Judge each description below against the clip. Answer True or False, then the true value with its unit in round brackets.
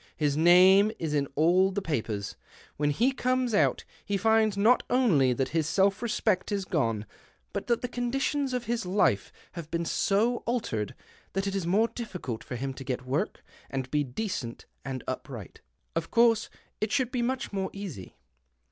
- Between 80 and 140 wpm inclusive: False (175 wpm)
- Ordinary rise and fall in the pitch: False (8.3 semitones)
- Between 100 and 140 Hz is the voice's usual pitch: False (190 Hz)